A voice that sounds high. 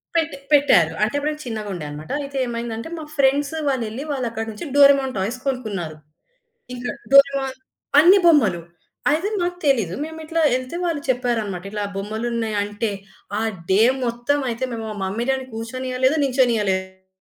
Yes: high, 240 Hz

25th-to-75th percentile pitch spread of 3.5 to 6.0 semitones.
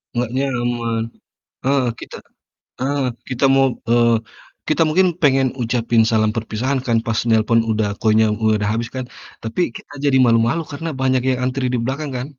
No: average, 3.0 semitones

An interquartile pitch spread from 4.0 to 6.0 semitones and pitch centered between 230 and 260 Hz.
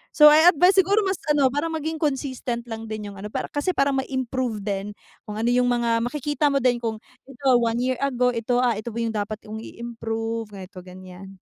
Yes: average, 4.3 semitones; high, 240 Hz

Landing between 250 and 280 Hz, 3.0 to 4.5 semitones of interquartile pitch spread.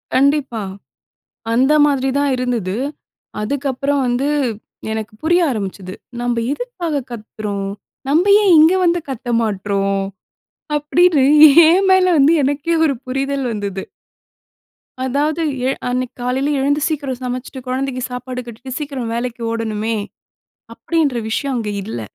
Yes: very high, 260 Hz; average, 4.0 semitones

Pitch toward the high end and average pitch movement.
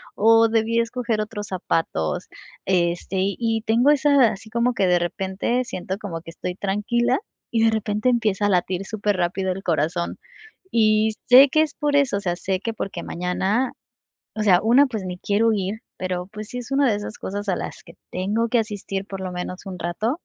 Yes: high, 210 Hz; average, 3.7 semitones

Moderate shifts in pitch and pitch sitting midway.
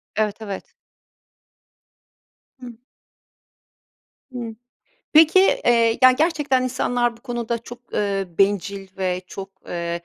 No: average, 4.1 semitones; high, 230 Hz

